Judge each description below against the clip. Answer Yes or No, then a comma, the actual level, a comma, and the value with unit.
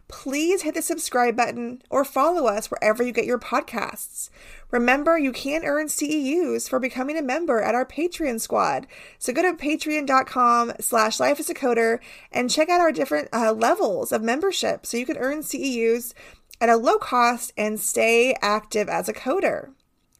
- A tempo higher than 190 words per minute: No, average, 175 wpm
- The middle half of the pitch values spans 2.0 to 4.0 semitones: No, average, 4.5 semitones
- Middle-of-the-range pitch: No, very high, 260 Hz